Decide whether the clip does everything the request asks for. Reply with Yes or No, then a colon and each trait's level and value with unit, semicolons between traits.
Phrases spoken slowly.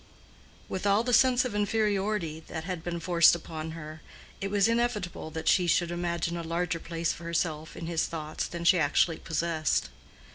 No: average, 180 wpm